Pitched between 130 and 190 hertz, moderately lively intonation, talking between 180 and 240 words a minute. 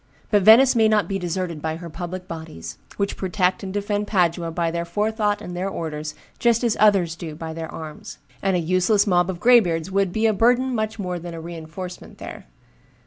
Yes: medium, 185 Hz; average, 3.8 semitones; average, 200 wpm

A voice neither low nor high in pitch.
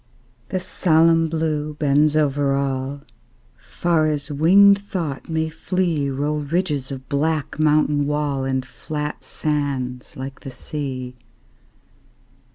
Yes: medium, 150 Hz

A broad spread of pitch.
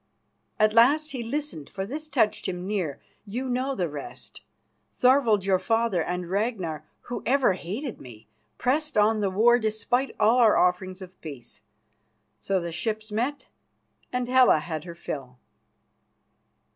Yes: wide, 5.7 semitones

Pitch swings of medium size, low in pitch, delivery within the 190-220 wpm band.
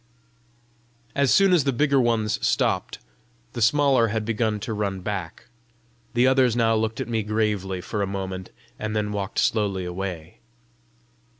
No: average, 3.4 semitones; low, 110 Hz; average, 155 wpm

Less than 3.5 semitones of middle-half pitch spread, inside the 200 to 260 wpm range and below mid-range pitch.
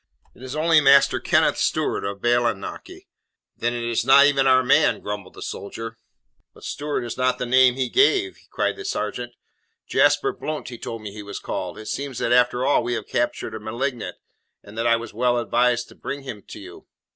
Yes: average, 2.9 semitones; fast, 205 wpm; low, 125 Hz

